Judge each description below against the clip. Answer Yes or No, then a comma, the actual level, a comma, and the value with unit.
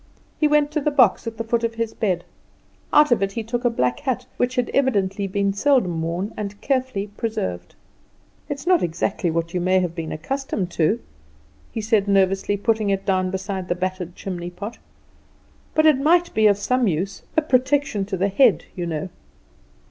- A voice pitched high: Yes, high, 200 Hz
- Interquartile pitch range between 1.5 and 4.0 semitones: No, average, 5.2 semitones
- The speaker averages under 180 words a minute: No, average, 185 wpm